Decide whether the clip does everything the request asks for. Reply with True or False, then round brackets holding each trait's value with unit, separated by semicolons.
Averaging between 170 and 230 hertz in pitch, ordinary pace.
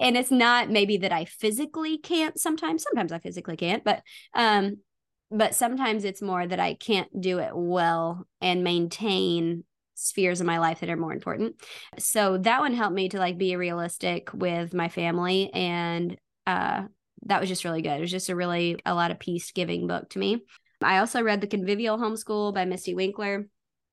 True (190 Hz; 190 wpm)